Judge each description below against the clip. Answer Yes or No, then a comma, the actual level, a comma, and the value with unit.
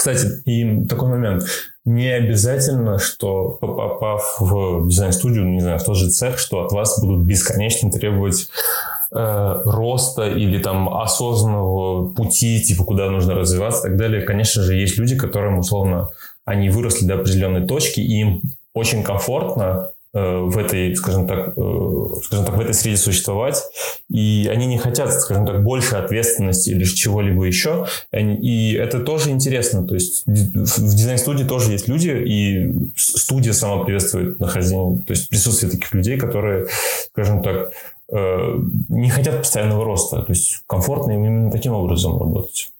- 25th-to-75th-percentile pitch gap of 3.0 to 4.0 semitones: Yes, average, 3.5 semitones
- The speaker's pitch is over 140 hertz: No, low, 105 Hz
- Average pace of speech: Yes, average, 150 wpm